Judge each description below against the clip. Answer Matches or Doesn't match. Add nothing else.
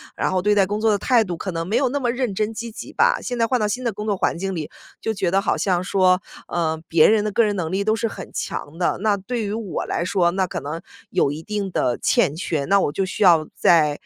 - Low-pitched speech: Doesn't match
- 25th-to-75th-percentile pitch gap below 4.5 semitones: Matches